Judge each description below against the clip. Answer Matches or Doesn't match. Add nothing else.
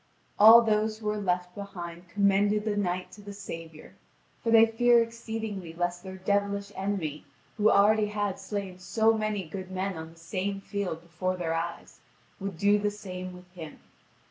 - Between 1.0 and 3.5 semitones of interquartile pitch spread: Matches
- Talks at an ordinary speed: Matches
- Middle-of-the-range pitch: Doesn't match